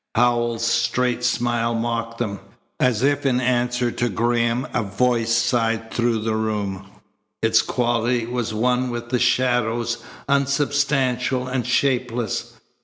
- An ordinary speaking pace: No, slow, 125 wpm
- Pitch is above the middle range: No, low, 120 Hz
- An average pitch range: No, narrow, 1.4 semitones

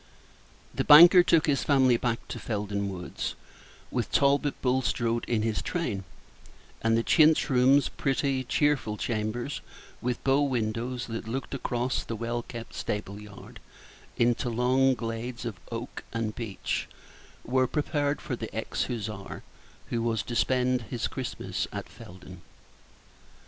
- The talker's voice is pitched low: Yes, low, 120 Hz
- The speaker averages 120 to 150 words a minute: Yes, average, 140 wpm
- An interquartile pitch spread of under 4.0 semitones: Yes, average, 2.9 semitones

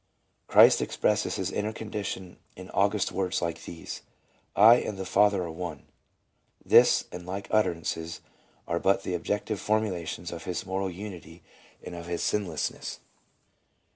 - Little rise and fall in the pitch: No, average, 3.1 semitones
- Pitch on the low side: Yes, very low, 95 Hz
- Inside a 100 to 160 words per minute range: Yes, average, 140 wpm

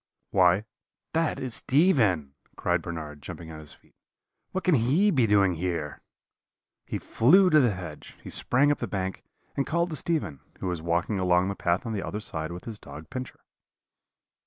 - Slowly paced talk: No, average, 180 wpm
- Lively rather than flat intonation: Yes, wide, 7.8 semitones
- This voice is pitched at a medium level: No, low, 100 Hz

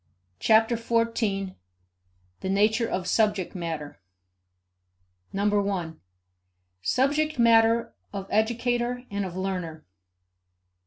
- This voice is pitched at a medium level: No, high, 210 Hz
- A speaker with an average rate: No, slow, 85 wpm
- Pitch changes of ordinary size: Yes, average, 3.5 semitones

